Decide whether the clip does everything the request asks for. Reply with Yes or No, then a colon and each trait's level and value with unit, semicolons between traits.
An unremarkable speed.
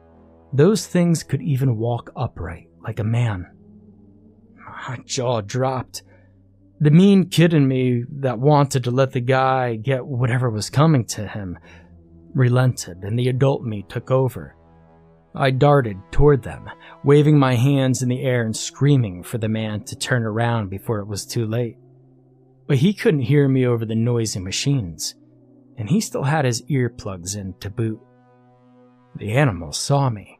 Yes: average, 160 wpm